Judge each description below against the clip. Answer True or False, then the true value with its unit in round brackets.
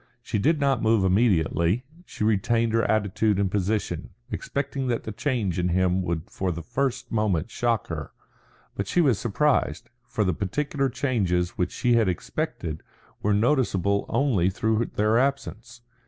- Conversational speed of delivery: True (155 wpm)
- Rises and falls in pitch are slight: False (4.7 semitones)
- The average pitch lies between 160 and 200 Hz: False (110 Hz)